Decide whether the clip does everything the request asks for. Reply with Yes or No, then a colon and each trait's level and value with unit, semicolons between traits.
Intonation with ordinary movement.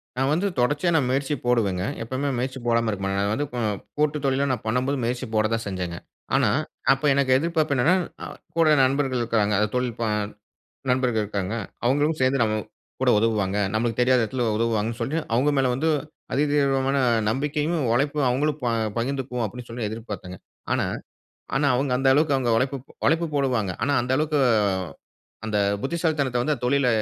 Yes: average, 3.7 semitones